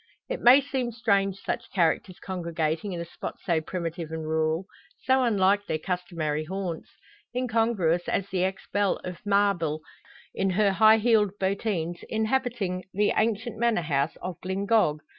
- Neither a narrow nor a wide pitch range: Yes, average, 4.4 semitones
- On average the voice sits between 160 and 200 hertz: Yes, high, 190 Hz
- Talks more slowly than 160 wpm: Yes, average, 150 wpm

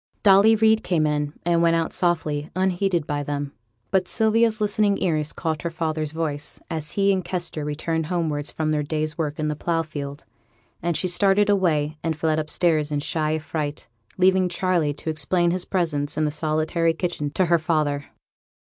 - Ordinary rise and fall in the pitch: Yes, average, 3.1 semitones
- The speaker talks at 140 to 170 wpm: No, average, 180 wpm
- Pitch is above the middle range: No, medium, 160 Hz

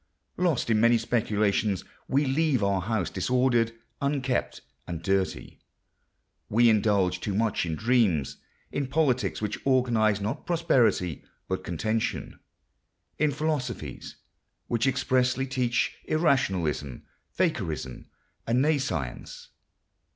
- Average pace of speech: No, slow, 105 wpm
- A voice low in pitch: Yes, low, 115 Hz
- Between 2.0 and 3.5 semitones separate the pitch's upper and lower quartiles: No, average, 5.2 semitones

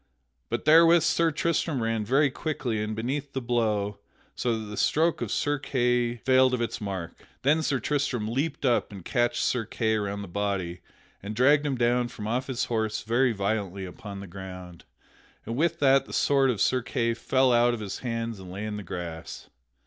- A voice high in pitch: No, low, 120 Hz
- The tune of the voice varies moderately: Yes, average, 4.3 semitones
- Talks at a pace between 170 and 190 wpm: No, average, 200 wpm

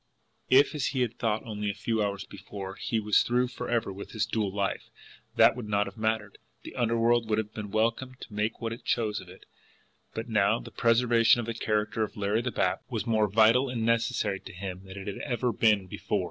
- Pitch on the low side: Yes, low, 110 Hz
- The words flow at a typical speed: No, fast, 220 wpm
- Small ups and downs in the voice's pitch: Yes, narrow, 2.2 semitones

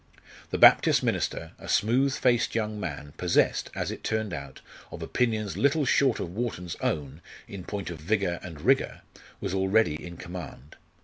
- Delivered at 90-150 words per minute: No, average, 165 wpm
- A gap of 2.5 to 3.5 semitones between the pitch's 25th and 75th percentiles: No, average, 5.1 semitones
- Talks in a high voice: No, very low, 95 Hz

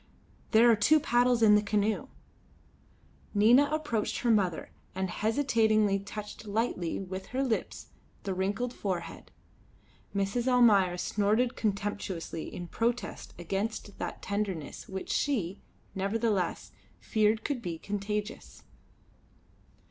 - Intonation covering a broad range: No, average, 3.2 semitones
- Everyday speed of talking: No, slow, 110 wpm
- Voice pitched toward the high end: Yes, high, 210 Hz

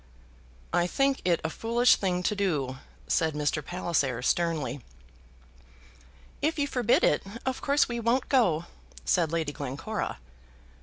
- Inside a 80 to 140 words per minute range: Yes, slow, 135 wpm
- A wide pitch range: Yes, wide, 8.0 semitones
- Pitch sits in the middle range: Yes, medium, 175 Hz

